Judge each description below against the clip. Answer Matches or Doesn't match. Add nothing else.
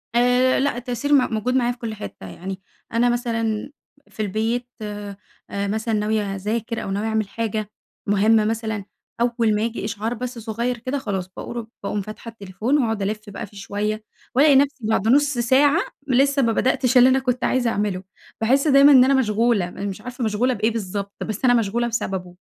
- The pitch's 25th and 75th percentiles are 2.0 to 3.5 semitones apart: Matches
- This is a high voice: Matches